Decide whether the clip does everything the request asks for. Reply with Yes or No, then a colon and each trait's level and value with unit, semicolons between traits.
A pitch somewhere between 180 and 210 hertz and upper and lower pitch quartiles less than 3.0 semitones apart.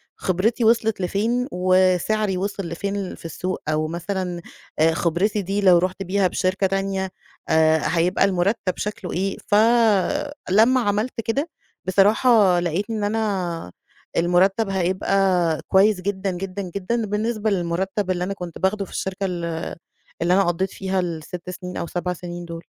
Yes: high, 190 Hz; narrow, 2.4 semitones